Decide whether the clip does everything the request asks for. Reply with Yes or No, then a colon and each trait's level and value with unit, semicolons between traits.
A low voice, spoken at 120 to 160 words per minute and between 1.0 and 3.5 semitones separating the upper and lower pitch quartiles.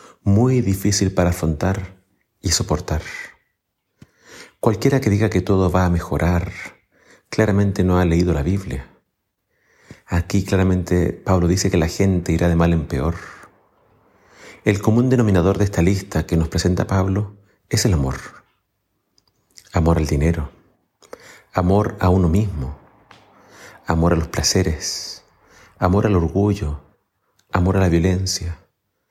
Yes: very low, 90 Hz; average, 130 wpm; average, 2.8 semitones